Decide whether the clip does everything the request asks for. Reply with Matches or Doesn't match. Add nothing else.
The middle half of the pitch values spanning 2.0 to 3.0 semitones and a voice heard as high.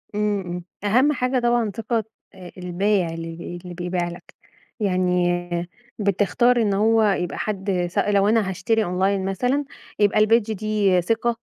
Doesn't match